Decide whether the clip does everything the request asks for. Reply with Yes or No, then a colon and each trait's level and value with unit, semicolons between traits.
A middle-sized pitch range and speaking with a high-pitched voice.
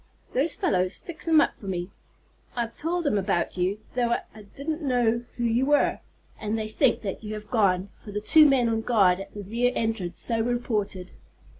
Yes: average, 3.8 semitones; high, 225 Hz